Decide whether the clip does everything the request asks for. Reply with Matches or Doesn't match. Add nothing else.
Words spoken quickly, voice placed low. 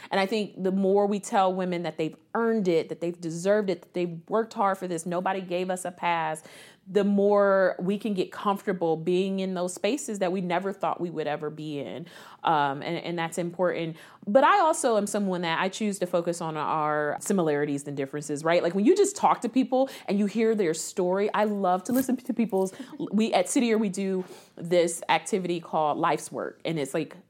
Doesn't match